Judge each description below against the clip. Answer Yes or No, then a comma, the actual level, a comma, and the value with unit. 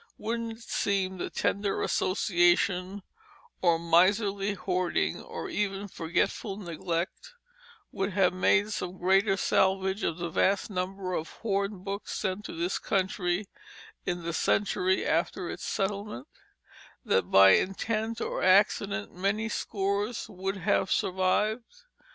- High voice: Yes, high, 195 Hz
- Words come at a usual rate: No, slow, 120 wpm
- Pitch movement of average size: No, narrow, 2.1 semitones